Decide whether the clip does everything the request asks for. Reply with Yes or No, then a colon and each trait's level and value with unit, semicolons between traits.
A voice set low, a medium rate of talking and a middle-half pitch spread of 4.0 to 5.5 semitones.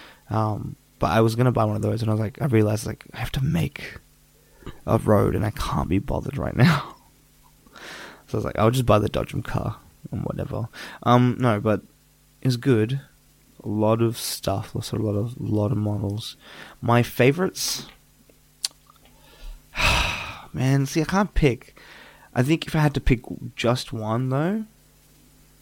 Yes: low, 115 Hz; average, 170 wpm; average, 4.3 semitones